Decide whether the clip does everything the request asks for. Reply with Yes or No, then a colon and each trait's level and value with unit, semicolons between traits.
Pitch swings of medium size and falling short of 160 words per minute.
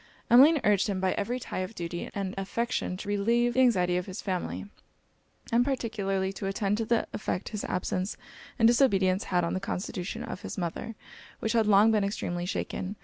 No: average, 3.6 semitones; average, 190 wpm